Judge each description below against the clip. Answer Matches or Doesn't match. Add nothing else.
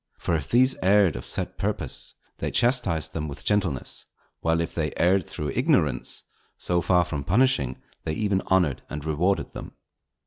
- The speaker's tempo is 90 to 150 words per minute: Doesn't match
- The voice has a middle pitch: Doesn't match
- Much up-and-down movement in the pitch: Doesn't match